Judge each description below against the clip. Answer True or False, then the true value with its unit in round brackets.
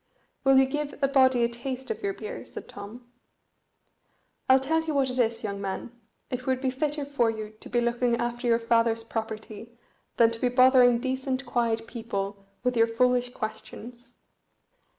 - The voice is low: False (245 Hz)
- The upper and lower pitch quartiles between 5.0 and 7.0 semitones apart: False (2.4 semitones)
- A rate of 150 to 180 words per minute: True (175 wpm)